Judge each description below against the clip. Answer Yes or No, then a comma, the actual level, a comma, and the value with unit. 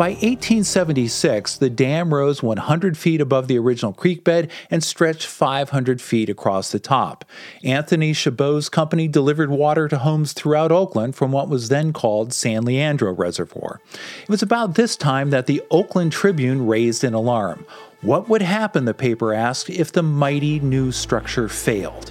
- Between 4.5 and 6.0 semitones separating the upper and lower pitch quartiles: Yes, average, 4.8 semitones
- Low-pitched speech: No, medium, 145 Hz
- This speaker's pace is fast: No, average, 165 wpm